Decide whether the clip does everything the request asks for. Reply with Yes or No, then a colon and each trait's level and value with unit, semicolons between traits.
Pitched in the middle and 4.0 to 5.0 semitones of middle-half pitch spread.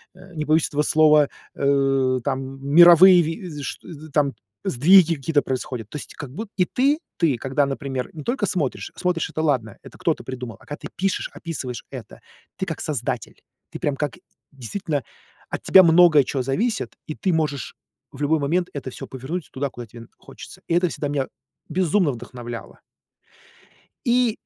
Yes: medium, 150 Hz; average, 4.6 semitones